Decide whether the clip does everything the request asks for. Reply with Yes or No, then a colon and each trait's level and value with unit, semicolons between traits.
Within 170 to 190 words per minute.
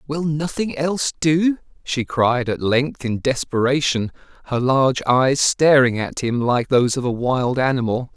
No: average, 160 wpm